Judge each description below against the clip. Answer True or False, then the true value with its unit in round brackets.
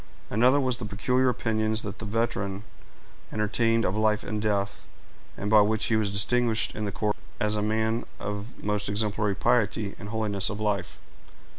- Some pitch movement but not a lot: False (1.6 semitones)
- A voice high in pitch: False (105 Hz)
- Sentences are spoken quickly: False (170 wpm)